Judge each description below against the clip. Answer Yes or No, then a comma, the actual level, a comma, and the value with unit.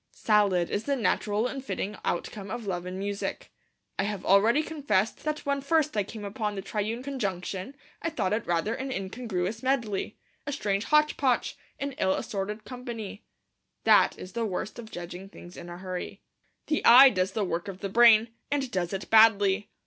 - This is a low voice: No, high, 210 Hz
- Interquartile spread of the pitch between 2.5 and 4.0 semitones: No, average, 4.5 semitones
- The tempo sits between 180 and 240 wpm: Yes, average, 185 wpm